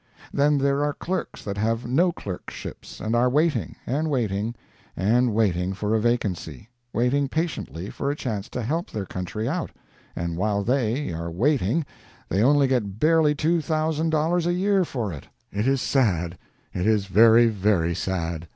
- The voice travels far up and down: Yes, wide, 6.8 semitones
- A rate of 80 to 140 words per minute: No, average, 170 wpm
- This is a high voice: No, low, 120 Hz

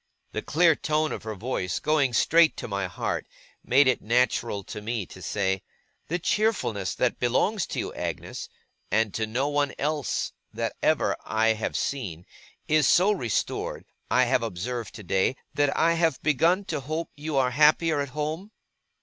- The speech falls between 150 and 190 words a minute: Yes, average, 165 wpm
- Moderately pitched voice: No, low, 130 Hz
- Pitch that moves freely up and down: Yes, wide, 5.9 semitones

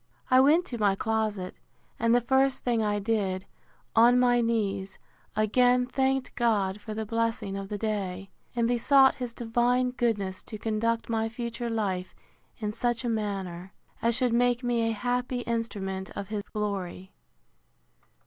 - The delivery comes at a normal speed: Yes, average, 155 wpm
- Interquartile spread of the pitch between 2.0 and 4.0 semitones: Yes, average, 3.1 semitones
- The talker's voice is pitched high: Yes, high, 225 Hz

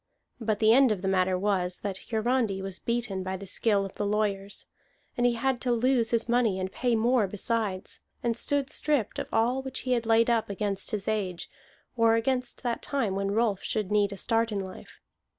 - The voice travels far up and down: No, average, 3.3 semitones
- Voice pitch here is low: No, high, 220 Hz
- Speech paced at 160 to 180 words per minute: No, fast, 205 wpm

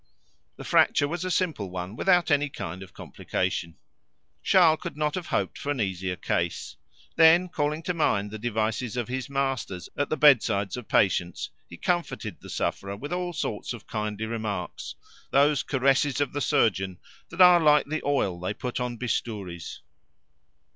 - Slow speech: No, average, 170 wpm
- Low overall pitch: Yes, low, 125 Hz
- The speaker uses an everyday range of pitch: No, wide, 6.9 semitones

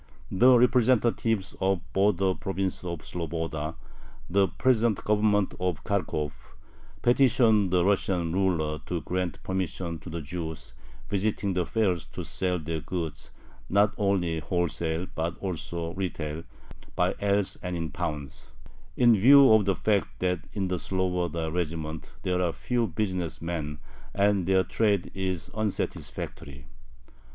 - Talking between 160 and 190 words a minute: No, slow, 135 wpm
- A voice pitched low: Yes, very low, 90 Hz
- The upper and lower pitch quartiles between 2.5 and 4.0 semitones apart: Yes, average, 3.5 semitones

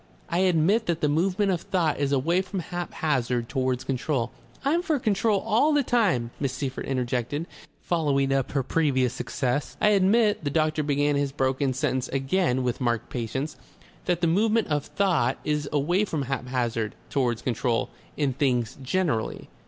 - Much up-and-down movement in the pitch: Yes, wide, 5.8 semitones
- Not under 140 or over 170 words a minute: Yes, average, 165 wpm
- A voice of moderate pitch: Yes, medium, 145 Hz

